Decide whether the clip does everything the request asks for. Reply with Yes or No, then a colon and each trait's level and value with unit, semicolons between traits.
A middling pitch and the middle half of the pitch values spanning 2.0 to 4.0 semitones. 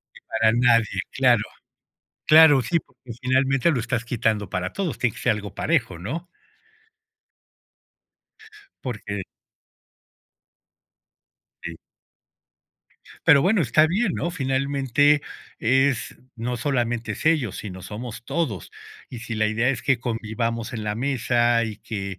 No: low, 120 Hz; average, 3.7 semitones